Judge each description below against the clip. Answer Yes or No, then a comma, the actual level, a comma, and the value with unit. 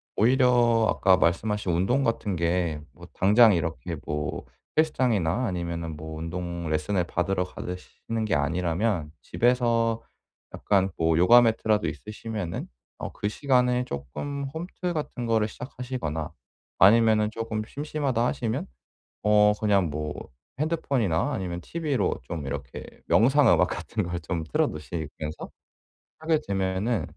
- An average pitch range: No, wide, 6.0 semitones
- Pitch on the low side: Yes, low, 105 Hz